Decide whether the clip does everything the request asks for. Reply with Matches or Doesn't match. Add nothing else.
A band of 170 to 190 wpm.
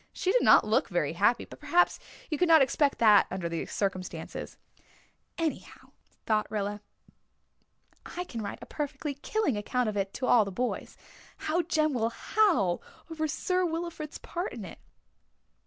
Doesn't match